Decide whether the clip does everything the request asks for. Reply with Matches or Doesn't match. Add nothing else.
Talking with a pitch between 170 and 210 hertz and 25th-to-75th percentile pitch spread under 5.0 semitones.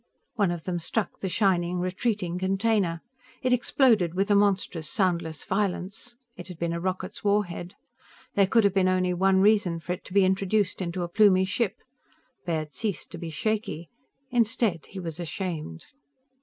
Matches